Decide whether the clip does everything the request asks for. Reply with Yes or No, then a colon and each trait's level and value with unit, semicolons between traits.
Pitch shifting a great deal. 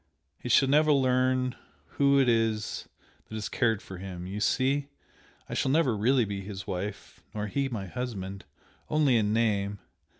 No: average, 4.7 semitones